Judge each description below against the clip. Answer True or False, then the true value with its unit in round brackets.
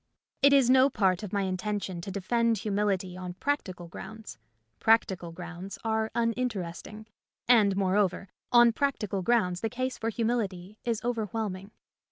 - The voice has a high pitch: True (210 Hz)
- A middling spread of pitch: True (3.8 semitones)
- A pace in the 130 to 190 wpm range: True (140 wpm)